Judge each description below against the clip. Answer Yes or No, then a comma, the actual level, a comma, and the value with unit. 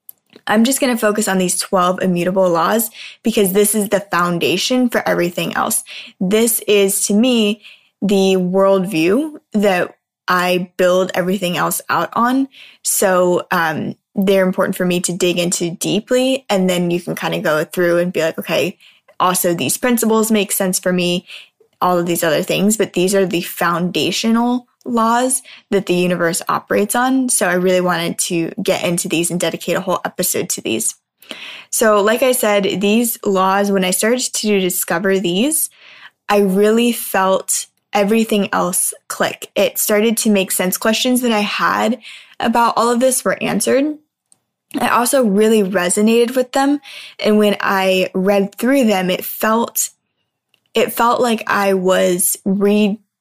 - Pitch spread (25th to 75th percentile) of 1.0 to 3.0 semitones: No, average, 3.8 semitones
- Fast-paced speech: No, average, 160 wpm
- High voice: Yes, high, 200 Hz